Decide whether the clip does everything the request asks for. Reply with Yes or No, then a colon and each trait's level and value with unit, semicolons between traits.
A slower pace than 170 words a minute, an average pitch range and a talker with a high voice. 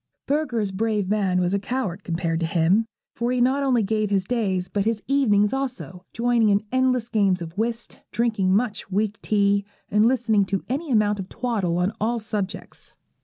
No: average, 180 wpm; average, 3.6 semitones; high, 210 Hz